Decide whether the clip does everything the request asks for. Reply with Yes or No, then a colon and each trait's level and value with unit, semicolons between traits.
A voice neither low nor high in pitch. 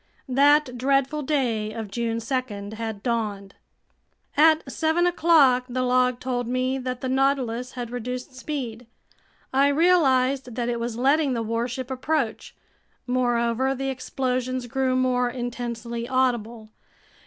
No: very high, 255 Hz